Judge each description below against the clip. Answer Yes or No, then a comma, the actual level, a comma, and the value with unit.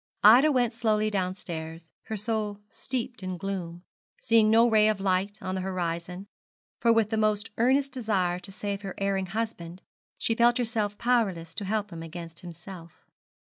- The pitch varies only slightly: No, average, 3.7 semitones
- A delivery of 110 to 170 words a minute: Yes, average, 165 wpm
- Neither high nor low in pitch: No, high, 205 Hz